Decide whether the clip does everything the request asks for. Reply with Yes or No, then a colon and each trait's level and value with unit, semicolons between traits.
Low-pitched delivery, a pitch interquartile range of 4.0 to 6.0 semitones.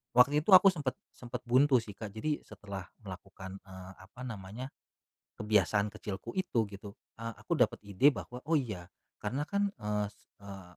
Yes: low, 110 Hz; average, 4.7 semitones